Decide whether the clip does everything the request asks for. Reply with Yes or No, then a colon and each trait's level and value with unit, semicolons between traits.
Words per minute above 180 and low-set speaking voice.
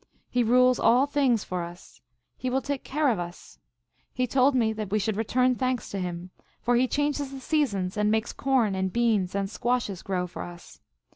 No: average, 200 wpm; high, 235 Hz